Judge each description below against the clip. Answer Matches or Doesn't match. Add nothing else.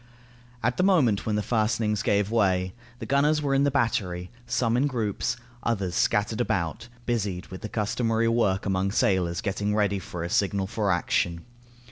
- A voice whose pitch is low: Matches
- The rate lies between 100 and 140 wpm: Doesn't match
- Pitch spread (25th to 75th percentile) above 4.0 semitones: Doesn't match